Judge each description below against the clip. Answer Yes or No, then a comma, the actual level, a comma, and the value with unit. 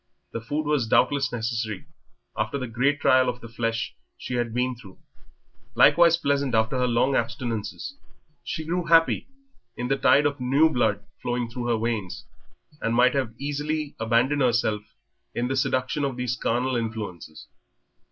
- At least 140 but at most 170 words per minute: Yes, average, 160 wpm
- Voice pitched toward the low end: Yes, low, 125 Hz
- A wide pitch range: No, average, 3.6 semitones